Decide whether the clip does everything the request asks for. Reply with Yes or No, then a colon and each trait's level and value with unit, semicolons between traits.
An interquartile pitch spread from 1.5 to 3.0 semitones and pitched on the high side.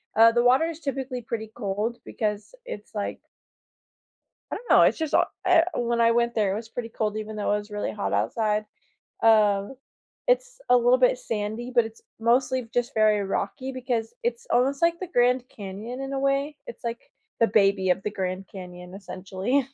No: average, 3.7 semitones; high, 230 Hz